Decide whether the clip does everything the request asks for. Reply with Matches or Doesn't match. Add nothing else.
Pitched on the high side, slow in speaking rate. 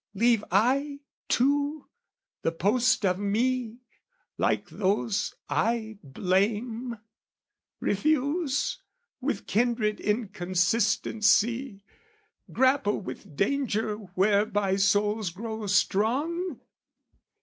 Matches